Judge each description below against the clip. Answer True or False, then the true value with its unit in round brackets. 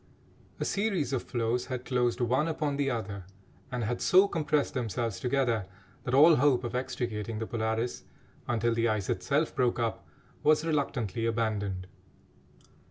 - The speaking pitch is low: True (120 Hz)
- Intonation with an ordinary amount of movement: True (3.8 semitones)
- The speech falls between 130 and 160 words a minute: True (150 wpm)